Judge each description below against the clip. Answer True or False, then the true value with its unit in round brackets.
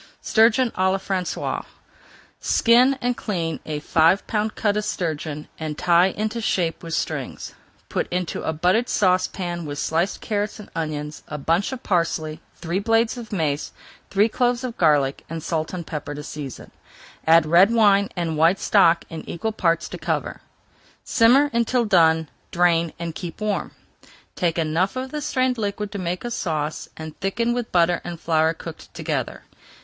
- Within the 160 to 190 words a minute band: True (170 wpm)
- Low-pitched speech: False (180 Hz)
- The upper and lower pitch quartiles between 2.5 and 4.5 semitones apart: False (5.0 semitones)